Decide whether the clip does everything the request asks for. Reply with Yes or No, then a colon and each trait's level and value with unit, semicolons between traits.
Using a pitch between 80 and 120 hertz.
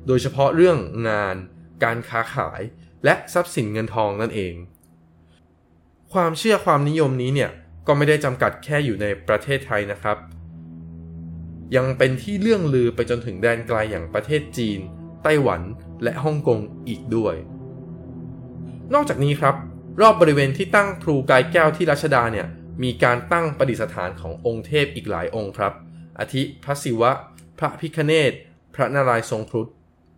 Yes: low, 115 Hz